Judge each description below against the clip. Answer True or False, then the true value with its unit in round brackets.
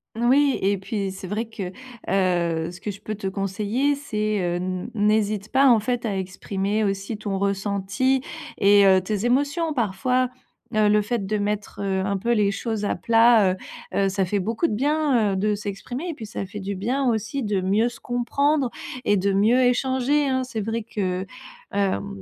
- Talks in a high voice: True (210 Hz)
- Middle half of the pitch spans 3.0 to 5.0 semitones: True (3.7 semitones)